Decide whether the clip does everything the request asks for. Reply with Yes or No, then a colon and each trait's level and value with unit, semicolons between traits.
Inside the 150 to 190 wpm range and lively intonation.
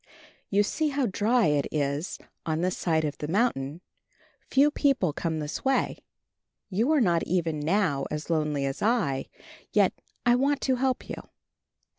Yes: average, 160 wpm; wide, 8.4 semitones